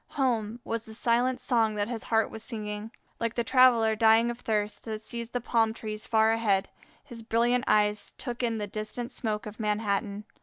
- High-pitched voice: Yes, high, 225 Hz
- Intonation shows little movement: Yes, narrow, 1.9 semitones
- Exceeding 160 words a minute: Yes, average, 190 wpm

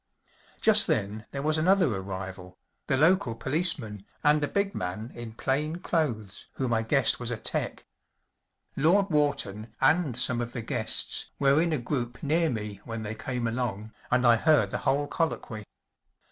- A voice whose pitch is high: No, low, 125 Hz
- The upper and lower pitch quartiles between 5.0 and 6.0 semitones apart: Yes, wide, 5.6 semitones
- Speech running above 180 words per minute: No, average, 160 wpm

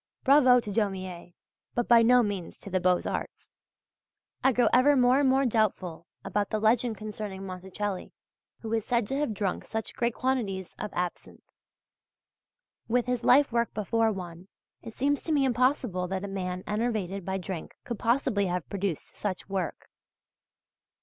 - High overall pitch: Yes, high, 215 Hz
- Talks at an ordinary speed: Yes, average, 165 wpm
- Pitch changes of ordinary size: Yes, average, 4.5 semitones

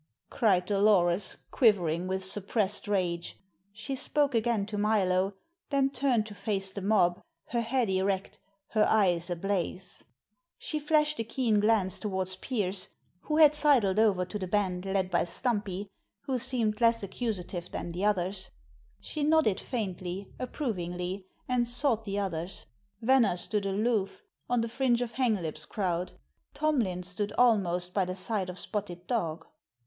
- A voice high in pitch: Yes, high, 205 Hz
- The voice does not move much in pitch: No, average, 4.1 semitones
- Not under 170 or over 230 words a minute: No, average, 145 wpm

